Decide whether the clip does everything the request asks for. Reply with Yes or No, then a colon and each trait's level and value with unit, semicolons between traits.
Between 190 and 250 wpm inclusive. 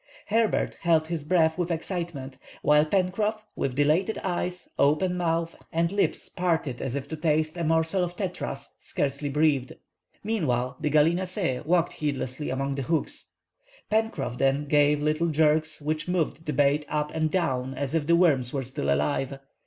No: average, 160 wpm